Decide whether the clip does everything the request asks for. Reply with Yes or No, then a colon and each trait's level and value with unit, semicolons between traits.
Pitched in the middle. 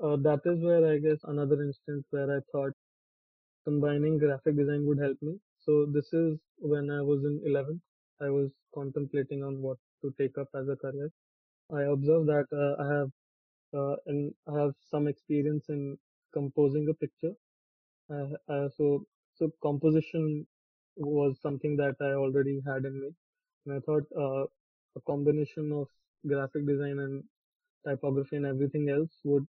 Yes: medium, 145 Hz